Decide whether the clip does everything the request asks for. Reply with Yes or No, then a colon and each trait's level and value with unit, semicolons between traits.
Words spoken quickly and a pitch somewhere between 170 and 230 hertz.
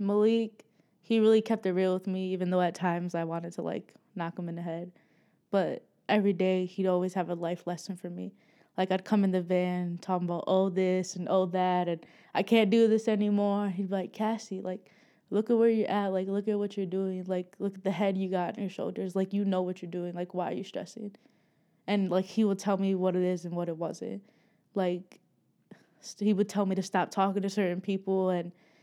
Yes: fast, 235 wpm; high, 190 Hz